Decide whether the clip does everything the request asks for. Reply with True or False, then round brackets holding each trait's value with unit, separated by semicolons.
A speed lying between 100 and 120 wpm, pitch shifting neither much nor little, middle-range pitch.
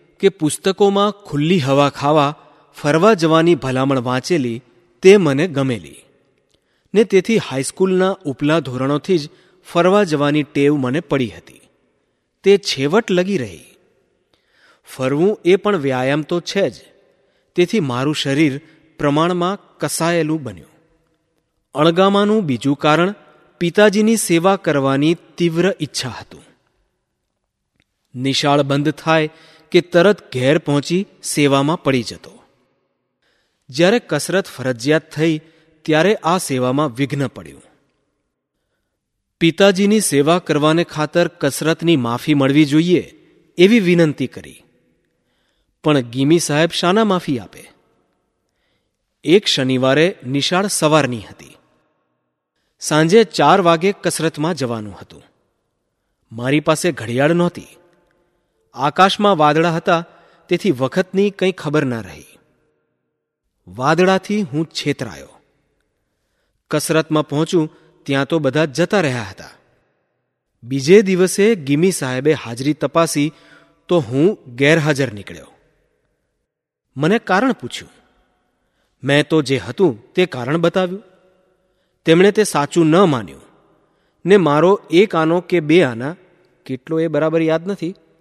True (105 wpm; 4.4 semitones; 160 Hz)